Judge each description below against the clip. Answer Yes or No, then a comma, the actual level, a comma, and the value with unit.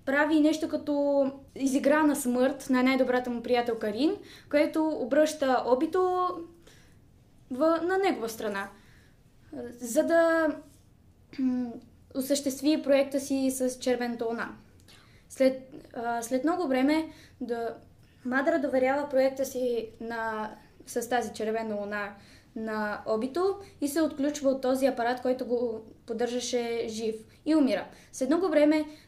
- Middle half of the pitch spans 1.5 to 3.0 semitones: No, average, 4.0 semitones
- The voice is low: No, very high, 265 Hz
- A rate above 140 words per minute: No, average, 120 wpm